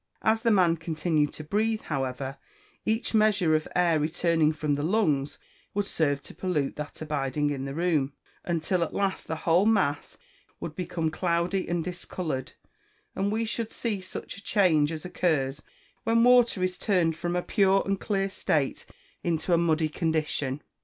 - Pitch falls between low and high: Yes, medium, 170 Hz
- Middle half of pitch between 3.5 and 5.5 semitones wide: Yes, average, 4.3 semitones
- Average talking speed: Yes, average, 165 wpm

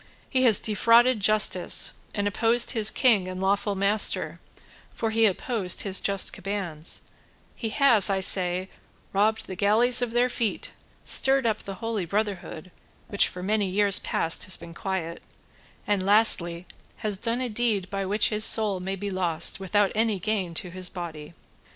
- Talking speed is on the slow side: No, average, 165 wpm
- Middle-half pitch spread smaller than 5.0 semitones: Yes, average, 2.9 semitones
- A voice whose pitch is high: Yes, high, 200 Hz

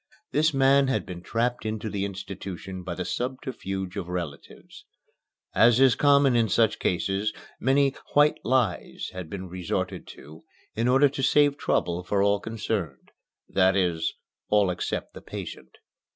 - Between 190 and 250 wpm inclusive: No, average, 150 wpm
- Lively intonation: Yes, wide, 6.1 semitones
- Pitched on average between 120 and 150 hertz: No, low, 105 Hz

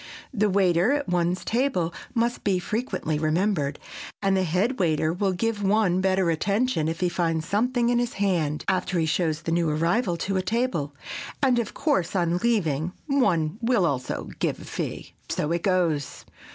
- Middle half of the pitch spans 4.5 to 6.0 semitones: Yes, average, 5.0 semitones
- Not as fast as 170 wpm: No, average, 175 wpm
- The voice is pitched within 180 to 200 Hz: Yes, medium, 185 Hz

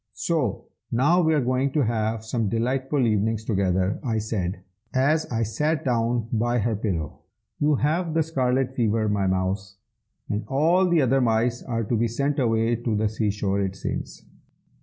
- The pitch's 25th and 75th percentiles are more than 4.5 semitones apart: No, average, 4.0 semitones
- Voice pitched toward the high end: No, low, 115 Hz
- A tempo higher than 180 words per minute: No, average, 175 wpm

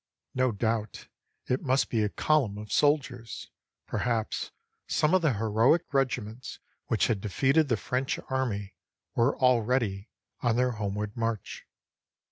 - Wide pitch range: No, average, 3.6 semitones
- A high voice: No, low, 120 Hz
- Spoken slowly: Yes, slow, 130 wpm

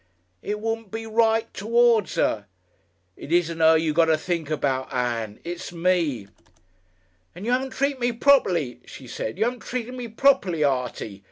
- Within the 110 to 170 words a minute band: Yes, average, 165 wpm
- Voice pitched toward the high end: No, medium, 175 Hz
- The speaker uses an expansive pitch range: Yes, wide, 7.9 semitones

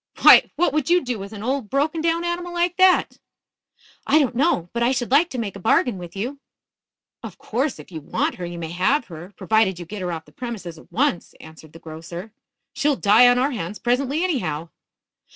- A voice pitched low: No, high, 235 Hz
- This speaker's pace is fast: Yes, fast, 220 wpm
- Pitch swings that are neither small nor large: No, wide, 8.3 semitones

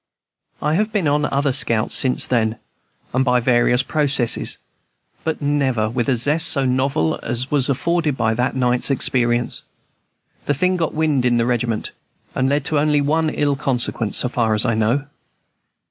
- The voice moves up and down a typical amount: Yes, average, 3.5 semitones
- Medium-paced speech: Yes, average, 175 wpm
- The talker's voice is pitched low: Yes, low, 130 Hz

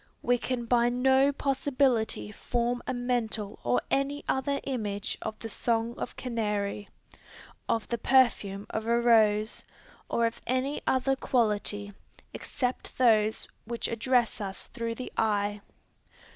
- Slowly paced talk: Yes, slow, 130 wpm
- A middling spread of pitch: Yes, average, 3.1 semitones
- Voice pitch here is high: Yes, high, 235 Hz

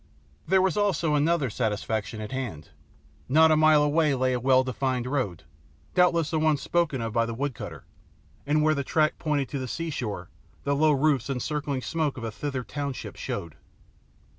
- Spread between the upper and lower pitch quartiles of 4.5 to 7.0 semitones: No, average, 3.8 semitones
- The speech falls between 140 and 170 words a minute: No, average, 185 wpm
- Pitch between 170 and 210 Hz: No, medium, 140 Hz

